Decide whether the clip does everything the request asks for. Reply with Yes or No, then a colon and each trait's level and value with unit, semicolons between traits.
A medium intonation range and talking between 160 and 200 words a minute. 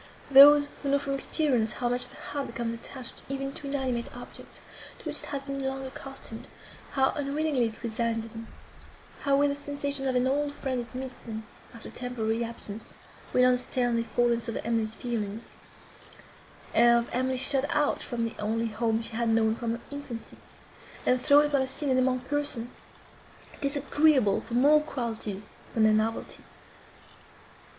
Yes: average, 3.3 semitones; average, 165 wpm